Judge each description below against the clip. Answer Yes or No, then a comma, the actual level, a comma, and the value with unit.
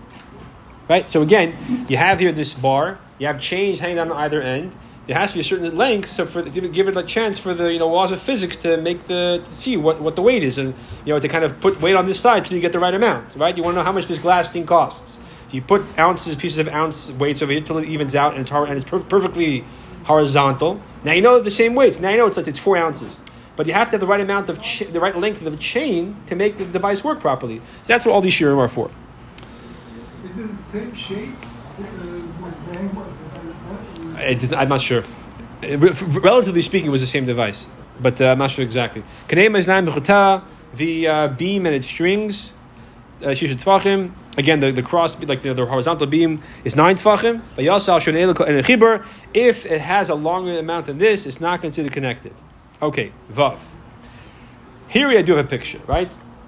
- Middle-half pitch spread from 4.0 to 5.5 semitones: Yes, average, 5.1 semitones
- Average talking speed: No, fast, 215 wpm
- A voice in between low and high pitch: Yes, medium, 170 Hz